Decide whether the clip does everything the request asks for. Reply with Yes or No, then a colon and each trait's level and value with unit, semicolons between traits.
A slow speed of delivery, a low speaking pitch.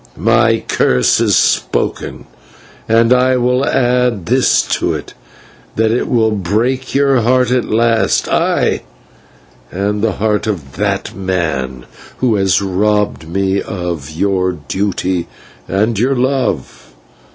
Yes: slow, 120 wpm; low, 105 Hz